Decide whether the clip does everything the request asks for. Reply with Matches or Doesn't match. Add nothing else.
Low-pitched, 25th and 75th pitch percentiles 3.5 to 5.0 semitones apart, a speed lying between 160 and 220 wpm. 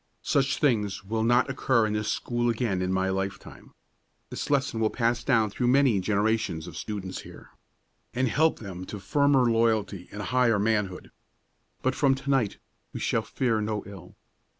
Matches